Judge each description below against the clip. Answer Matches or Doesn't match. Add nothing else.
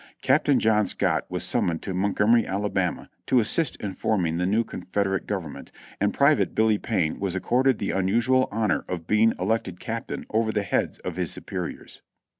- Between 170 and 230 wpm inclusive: Matches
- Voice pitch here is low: Matches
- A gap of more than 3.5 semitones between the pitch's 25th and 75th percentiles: Doesn't match